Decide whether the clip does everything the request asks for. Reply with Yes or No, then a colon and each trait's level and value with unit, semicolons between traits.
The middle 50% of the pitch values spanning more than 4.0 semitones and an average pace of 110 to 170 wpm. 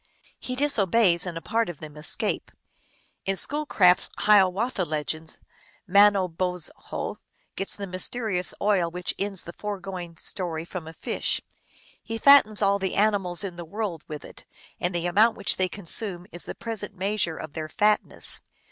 No: average, 3.3 semitones; average, 165 wpm